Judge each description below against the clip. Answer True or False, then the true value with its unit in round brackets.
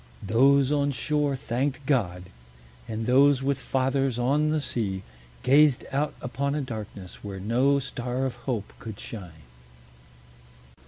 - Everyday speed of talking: False (130 wpm)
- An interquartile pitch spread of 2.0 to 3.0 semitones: False (3.8 semitones)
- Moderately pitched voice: False (130 Hz)